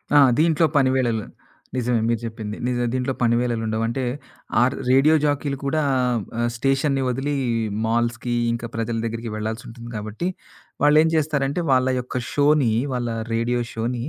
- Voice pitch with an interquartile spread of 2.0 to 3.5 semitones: Yes, average, 3.0 semitones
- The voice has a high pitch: No, low, 125 Hz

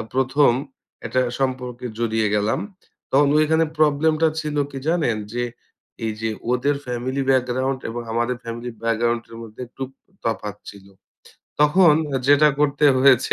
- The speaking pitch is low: Yes, low, 130 Hz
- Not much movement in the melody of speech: No, average, 3.6 semitones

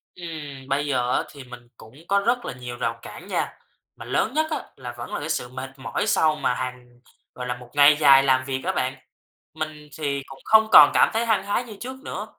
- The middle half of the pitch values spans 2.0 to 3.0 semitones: No, average, 4.6 semitones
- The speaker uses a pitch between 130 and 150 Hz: Yes, medium, 140 Hz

